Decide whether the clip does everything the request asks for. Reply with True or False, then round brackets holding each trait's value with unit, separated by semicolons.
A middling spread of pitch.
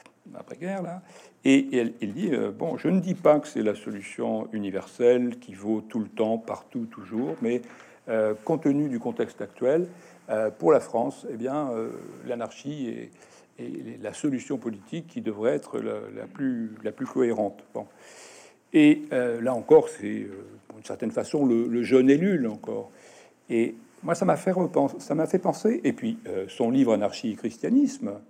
False (8.6 semitones)